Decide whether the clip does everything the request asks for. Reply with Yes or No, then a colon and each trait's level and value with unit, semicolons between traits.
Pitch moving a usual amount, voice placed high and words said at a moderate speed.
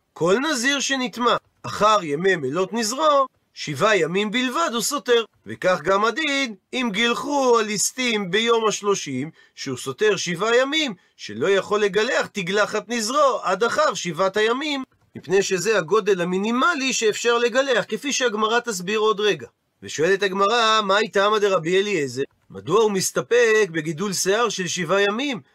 Yes: average, 3.8 semitones; high, 215 Hz; average, 140 wpm